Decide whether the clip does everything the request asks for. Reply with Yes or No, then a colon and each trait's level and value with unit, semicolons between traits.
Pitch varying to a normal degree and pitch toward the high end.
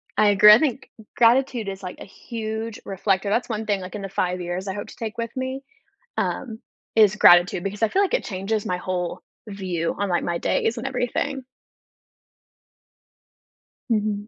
Yes: average, 3.5 semitones; high, 210 Hz